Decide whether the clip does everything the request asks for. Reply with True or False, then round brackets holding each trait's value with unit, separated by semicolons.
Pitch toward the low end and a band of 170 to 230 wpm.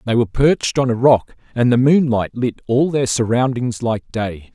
True (120 Hz; 200 wpm)